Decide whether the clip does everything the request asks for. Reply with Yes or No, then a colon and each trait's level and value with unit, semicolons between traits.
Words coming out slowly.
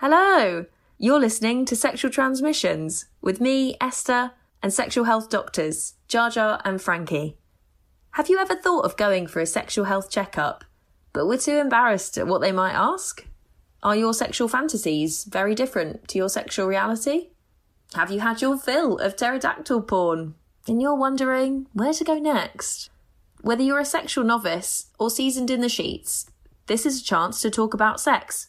No: average, 170 wpm